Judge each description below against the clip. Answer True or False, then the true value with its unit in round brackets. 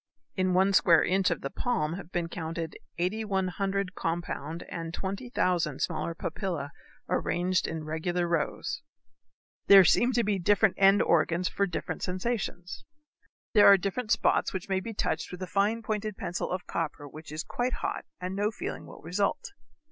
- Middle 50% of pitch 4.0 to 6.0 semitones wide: False (3.0 semitones)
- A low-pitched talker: False (185 Hz)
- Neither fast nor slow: True (165 wpm)